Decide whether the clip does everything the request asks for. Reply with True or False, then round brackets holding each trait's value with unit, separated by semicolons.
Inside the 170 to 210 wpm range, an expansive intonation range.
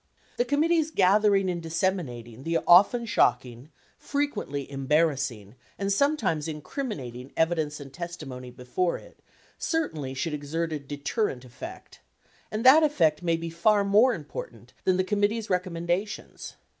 False (135 wpm; 6.7 semitones)